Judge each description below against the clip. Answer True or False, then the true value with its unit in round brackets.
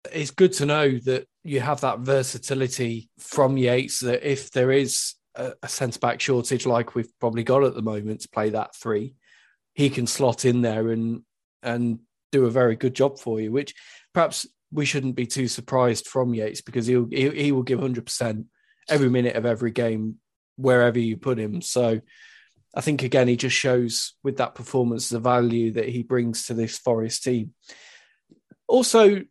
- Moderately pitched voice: False (125 Hz)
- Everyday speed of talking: True (185 wpm)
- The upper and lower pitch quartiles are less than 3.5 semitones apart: True (2.5 semitones)